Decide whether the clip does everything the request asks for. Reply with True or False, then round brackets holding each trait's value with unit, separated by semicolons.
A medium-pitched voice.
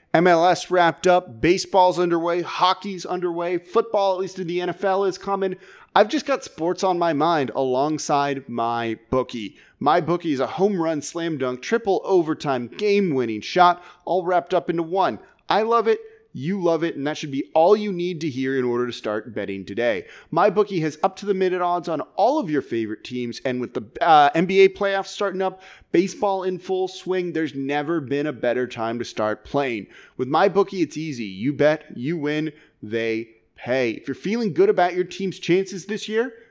True (175 Hz)